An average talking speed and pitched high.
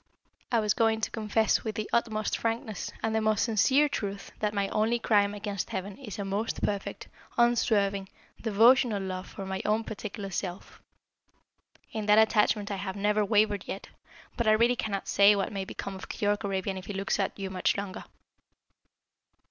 Yes: average, 180 wpm; high, 210 Hz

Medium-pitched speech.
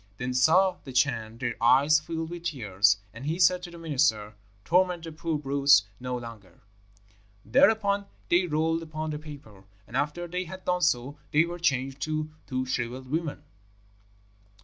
Yes: medium, 150 Hz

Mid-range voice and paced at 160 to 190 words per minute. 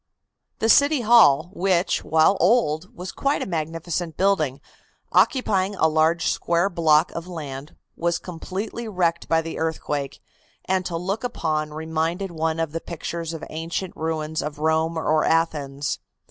No: medium, 165 Hz; average, 145 wpm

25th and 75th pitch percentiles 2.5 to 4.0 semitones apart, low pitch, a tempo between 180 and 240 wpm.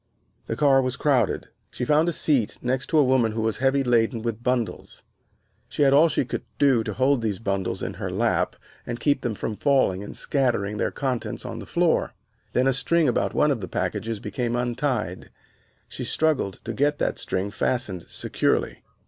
Yes: average, 3.7 semitones; low, 125 Hz; average, 190 wpm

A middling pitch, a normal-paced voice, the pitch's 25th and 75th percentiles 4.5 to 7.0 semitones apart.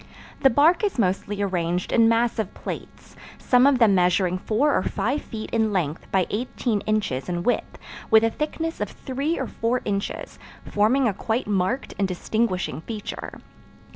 No: high, 220 Hz; average, 165 wpm; average, 4.8 semitones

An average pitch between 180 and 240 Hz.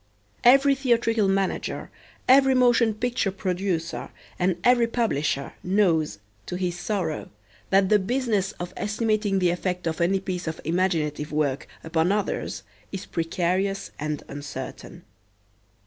Yes: high, 190 Hz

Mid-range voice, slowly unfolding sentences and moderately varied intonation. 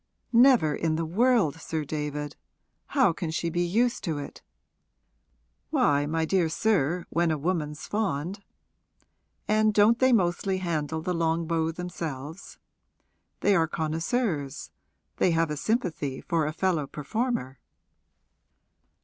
Yes: medium, 165 Hz; slow, 130 wpm; average, 4.3 semitones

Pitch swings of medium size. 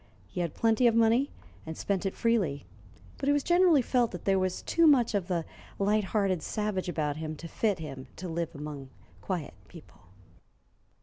No: wide, 6.0 semitones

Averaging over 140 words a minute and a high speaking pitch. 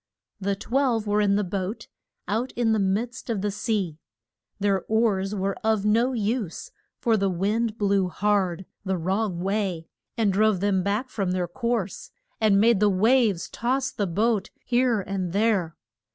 Yes: average, 165 wpm; high, 205 Hz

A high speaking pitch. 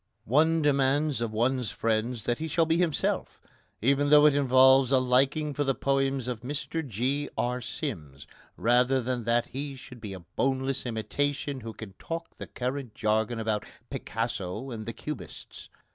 No: low, 130 Hz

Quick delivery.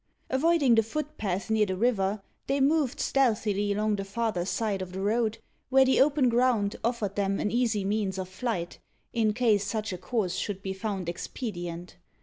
No: average, 175 wpm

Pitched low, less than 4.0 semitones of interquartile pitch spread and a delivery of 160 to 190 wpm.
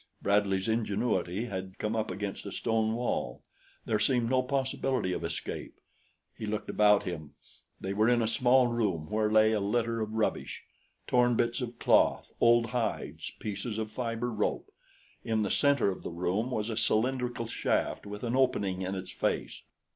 Yes: low, 110 Hz; average, 2.9 semitones; average, 170 wpm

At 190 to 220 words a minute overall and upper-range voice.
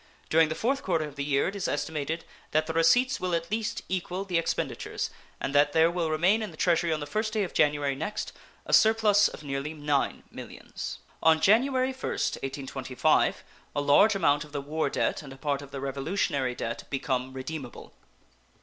No: average, 195 wpm; medium, 155 Hz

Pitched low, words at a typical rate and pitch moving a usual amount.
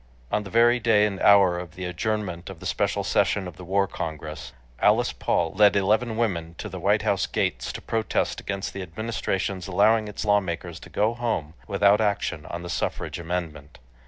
Yes: very low, 95 Hz; average, 190 wpm; average, 3.6 semitones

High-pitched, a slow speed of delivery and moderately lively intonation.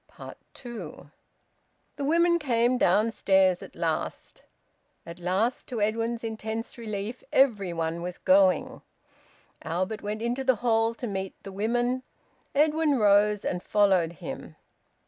Yes: high, 215 Hz; slow, 125 wpm; average, 4.1 semitones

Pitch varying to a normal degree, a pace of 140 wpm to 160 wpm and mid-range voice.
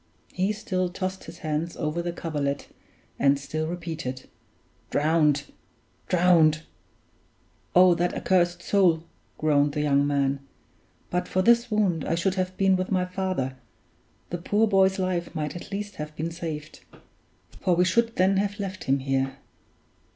Yes: average, 3.7 semitones; average, 150 wpm; medium, 175 Hz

